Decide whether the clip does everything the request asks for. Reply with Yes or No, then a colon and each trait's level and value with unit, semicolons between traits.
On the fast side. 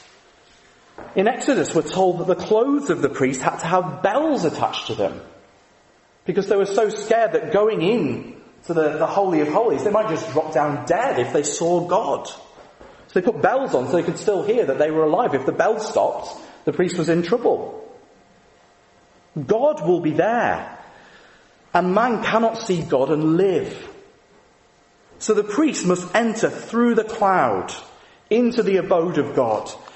No: average, 175 wpm